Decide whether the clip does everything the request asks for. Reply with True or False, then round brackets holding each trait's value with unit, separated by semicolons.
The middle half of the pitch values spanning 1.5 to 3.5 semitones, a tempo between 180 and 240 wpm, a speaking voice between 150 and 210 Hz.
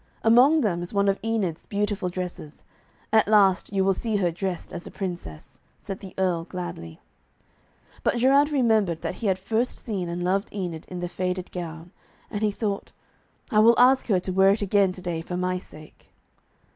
True (3.1 semitones; 190 wpm; 190 Hz)